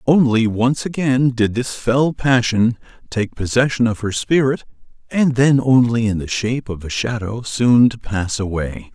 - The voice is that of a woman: No, male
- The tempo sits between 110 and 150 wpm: No, average, 170 wpm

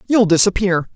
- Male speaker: No, female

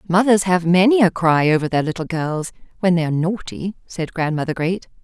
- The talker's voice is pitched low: No, medium, 175 Hz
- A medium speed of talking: Yes, average, 190 wpm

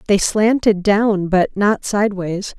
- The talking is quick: No, average, 140 wpm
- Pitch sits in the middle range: No, high, 200 Hz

